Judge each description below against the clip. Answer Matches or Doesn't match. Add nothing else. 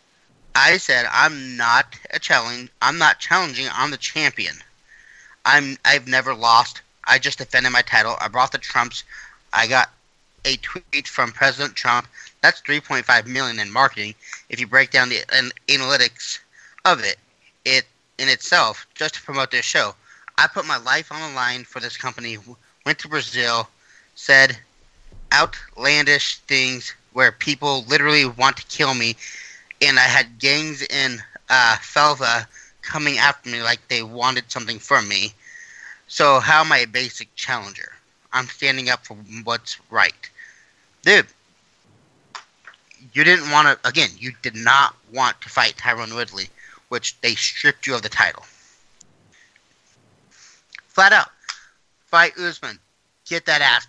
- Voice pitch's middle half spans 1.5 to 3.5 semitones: Matches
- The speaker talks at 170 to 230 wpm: Doesn't match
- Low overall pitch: Matches